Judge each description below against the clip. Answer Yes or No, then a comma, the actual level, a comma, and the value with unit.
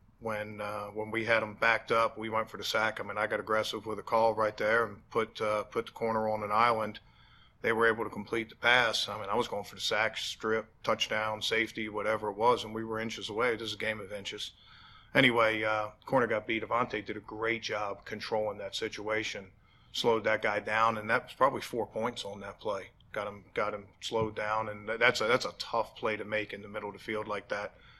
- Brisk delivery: Yes, fast, 240 wpm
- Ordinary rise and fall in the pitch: No, narrow, 1.0 semitones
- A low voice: Yes, low, 110 Hz